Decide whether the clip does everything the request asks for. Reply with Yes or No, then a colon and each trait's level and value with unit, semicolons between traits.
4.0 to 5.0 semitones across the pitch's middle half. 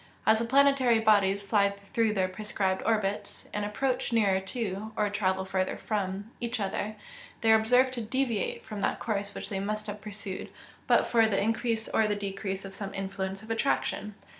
No: narrow, 2.4 semitones